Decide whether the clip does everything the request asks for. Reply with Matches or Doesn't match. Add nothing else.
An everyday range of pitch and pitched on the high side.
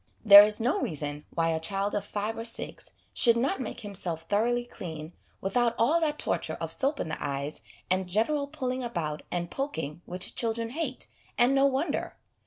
Doesn't match